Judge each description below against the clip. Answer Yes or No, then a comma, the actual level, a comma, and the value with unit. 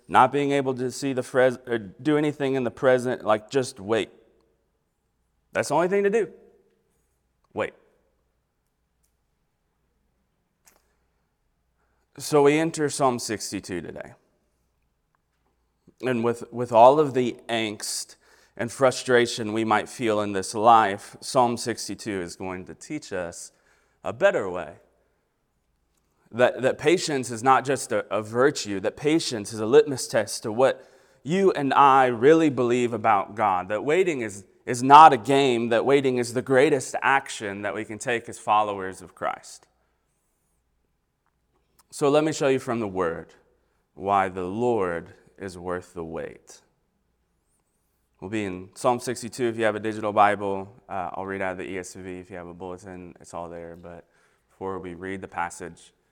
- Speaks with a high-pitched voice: No, low, 115 Hz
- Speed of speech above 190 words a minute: No, average, 155 wpm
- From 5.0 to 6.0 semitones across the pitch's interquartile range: Yes, wide, 5.5 semitones